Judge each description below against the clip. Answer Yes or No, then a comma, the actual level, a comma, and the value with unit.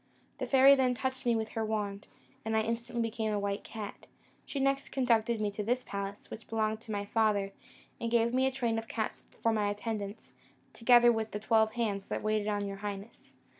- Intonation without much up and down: Yes, narrow, 2.2 semitones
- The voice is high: Yes, high, 220 Hz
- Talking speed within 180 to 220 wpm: Yes, fast, 205 wpm